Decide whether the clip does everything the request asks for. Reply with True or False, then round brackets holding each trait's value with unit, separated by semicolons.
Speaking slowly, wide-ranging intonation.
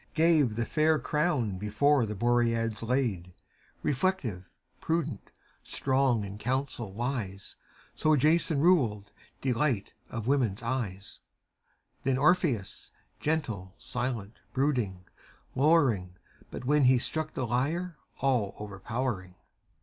True (105 wpm; 5.7 semitones)